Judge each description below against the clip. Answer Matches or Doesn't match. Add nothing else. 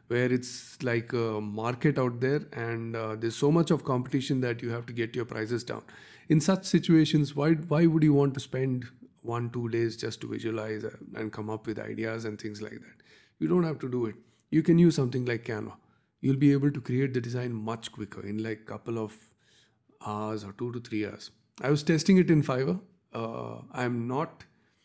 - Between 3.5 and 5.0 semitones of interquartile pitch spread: Matches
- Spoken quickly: Matches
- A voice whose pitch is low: Matches